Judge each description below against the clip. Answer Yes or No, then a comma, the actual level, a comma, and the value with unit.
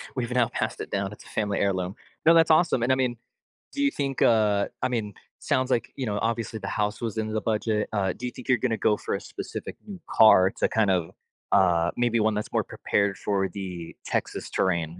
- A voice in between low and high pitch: No, low, 110 Hz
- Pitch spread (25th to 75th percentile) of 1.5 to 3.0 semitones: No, average, 3.7 semitones